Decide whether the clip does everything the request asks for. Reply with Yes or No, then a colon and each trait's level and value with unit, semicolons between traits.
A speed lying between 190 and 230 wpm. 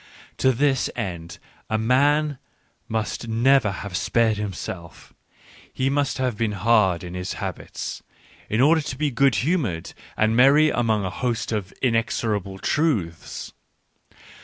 No: slow, 135 wpm